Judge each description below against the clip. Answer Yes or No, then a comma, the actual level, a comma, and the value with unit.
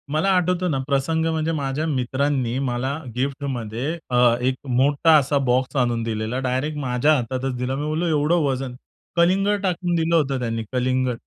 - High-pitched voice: No, low, 135 Hz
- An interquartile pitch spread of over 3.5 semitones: Yes, average, 4.0 semitones